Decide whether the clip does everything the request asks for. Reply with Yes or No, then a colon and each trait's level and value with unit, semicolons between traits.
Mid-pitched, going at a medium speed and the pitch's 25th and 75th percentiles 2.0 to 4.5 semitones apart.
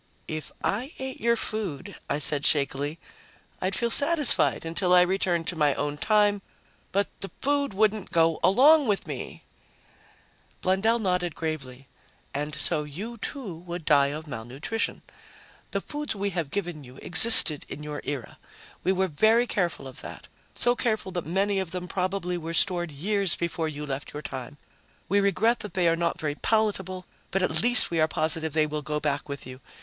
No: medium, 175 Hz; average, 180 wpm; average, 5.2 semitones